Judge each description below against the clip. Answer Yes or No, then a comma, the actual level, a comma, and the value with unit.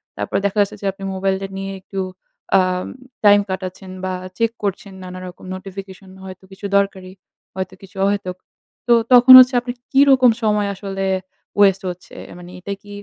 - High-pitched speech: Yes, high, 195 Hz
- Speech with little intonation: Yes, narrow, 1.5 semitones